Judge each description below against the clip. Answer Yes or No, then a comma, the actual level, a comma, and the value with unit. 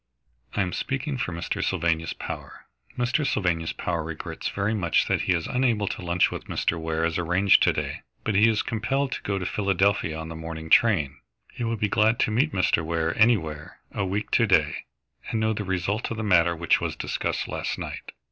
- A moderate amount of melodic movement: Yes, average, 5.0 semitones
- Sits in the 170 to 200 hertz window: No, very low, 95 Hz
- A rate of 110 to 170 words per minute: No, fast, 205 wpm